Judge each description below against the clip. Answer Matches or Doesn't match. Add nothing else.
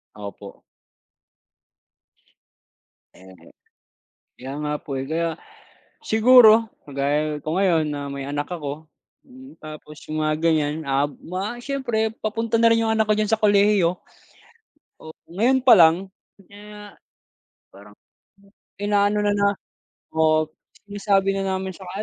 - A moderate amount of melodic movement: Doesn't match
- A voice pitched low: Doesn't match